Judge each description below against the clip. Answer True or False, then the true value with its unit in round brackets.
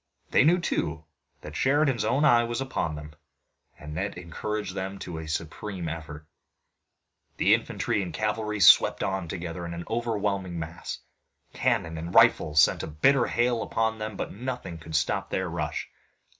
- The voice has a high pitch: False (95 Hz)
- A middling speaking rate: True (155 wpm)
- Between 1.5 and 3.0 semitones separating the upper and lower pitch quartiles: False (5.6 semitones)